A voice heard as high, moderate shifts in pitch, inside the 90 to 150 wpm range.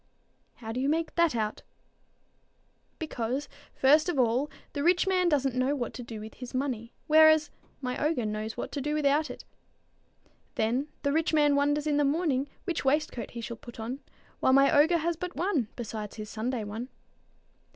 No: very high, 275 Hz; average, 4.5 semitones; average, 180 wpm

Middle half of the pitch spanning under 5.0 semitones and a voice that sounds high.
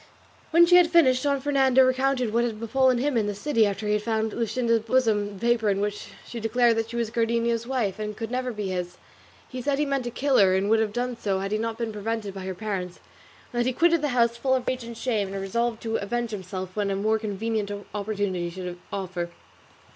Yes: average, 3.5 semitones; high, 225 Hz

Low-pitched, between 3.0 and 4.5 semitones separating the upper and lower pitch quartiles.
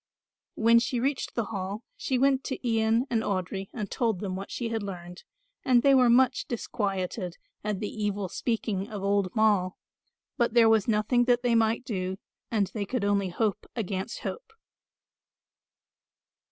No: high, 220 Hz; average, 3.4 semitones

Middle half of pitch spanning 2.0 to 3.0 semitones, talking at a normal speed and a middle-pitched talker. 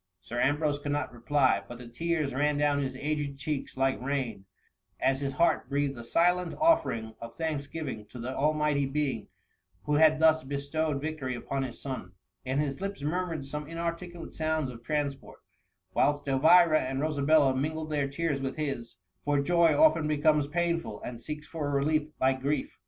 Yes: average, 2.7 semitones; average, 180 wpm; medium, 145 Hz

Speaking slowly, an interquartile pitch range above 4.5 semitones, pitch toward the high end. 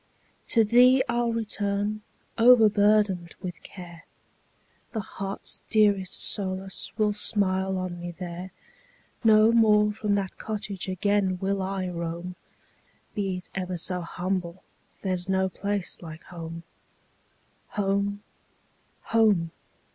No: slow, 105 wpm; narrow, 2.6 semitones; high, 195 Hz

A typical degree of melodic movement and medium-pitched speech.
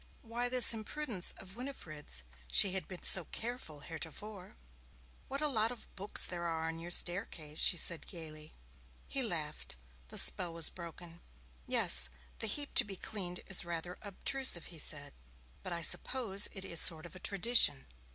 Yes: average, 5.0 semitones; medium, 180 Hz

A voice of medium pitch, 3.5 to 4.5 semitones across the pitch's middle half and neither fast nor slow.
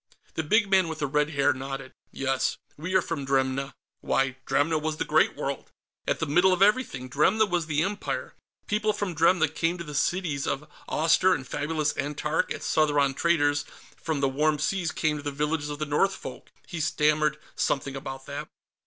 No: medium, 150 Hz; average, 3.0 semitones; average, 190 wpm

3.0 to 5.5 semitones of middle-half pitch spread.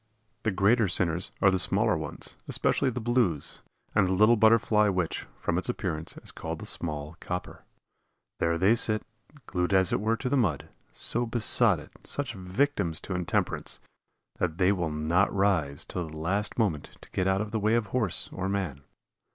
Yes: average, 4.3 semitones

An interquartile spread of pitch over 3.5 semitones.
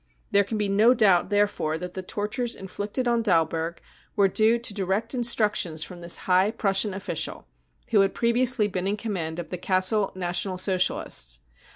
No: average, 3.2 semitones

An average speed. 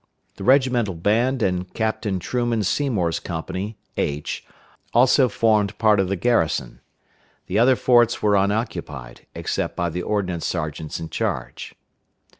No: slow, 130 wpm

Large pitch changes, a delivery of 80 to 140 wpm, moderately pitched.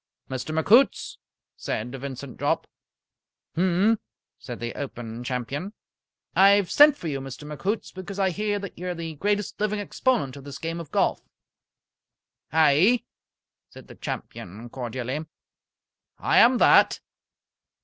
Yes: wide, 7.2 semitones; slow, 135 wpm; medium, 160 Hz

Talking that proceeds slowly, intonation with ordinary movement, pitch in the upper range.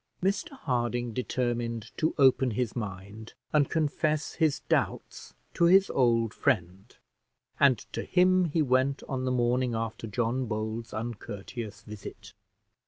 No: slow, 130 wpm; average, 4.0 semitones; low, 120 Hz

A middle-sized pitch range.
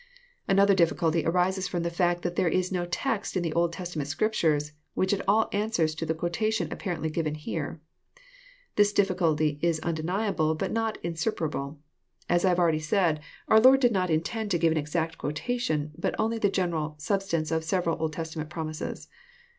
Yes: average, 3.6 semitones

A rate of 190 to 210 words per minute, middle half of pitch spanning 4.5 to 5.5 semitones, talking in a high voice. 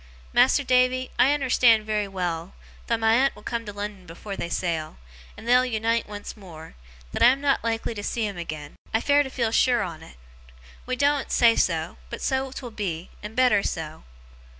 Yes: average, 195 wpm; average, 4.8 semitones; high, 225 Hz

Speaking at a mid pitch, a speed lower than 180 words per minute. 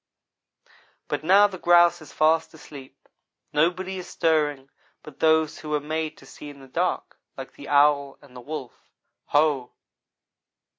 Yes: medium, 155 Hz; average, 150 wpm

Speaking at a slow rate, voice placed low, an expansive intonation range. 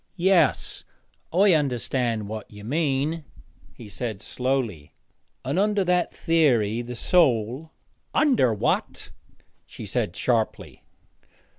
Yes: slow, 110 wpm; low, 130 Hz; wide, 6.7 semitones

